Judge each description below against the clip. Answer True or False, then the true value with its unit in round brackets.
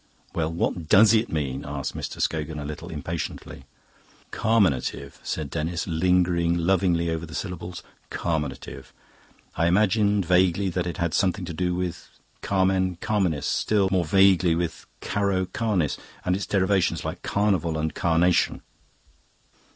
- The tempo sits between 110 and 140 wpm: True (135 wpm)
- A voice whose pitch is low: True (90 Hz)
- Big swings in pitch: False (2.8 semitones)